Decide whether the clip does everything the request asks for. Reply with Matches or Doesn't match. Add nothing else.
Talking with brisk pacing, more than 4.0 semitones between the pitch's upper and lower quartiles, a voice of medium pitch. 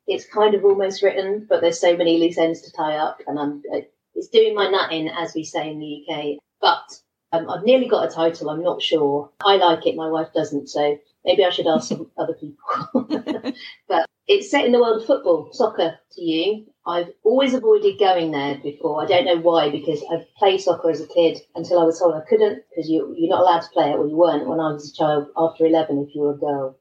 Matches